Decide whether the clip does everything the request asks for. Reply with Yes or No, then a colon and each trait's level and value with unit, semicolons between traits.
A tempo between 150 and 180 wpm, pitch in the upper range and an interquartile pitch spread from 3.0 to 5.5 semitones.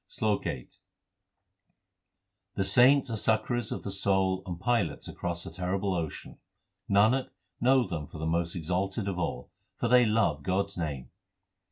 No: average, 155 wpm; very low, 95 Hz; average, 4.4 semitones